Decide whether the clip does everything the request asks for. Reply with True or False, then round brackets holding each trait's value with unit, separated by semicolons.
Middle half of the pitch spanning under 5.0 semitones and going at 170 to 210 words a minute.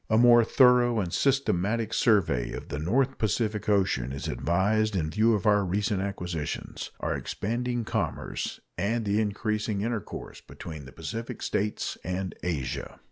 False (4.4 semitones; 145 wpm)